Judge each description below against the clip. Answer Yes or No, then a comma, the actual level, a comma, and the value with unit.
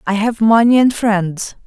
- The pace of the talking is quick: No, average, 180 wpm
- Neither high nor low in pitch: No, high, 215 Hz